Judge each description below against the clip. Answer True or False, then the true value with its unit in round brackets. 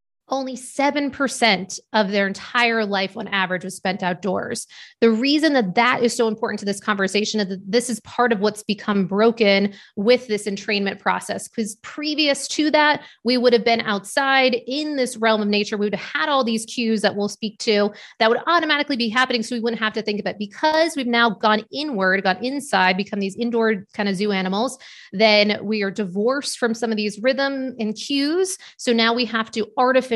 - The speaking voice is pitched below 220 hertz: False (225 Hz)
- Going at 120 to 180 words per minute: False (205 wpm)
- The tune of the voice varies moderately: True (3.7 semitones)